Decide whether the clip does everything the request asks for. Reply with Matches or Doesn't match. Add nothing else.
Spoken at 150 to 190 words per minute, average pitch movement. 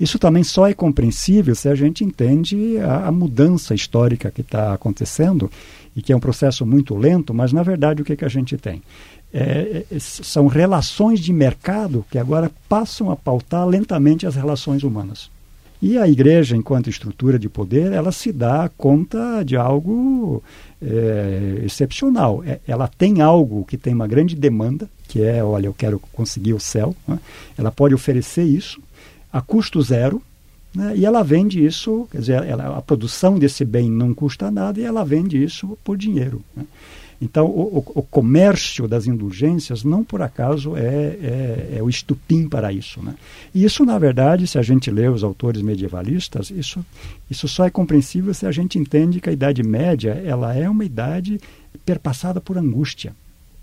Doesn't match